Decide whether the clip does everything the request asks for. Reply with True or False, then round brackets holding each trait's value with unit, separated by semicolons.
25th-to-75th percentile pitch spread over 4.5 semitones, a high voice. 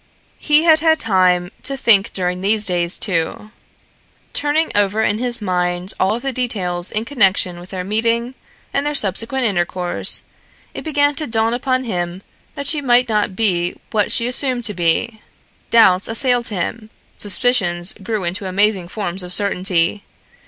True (5.1 semitones; 210 Hz)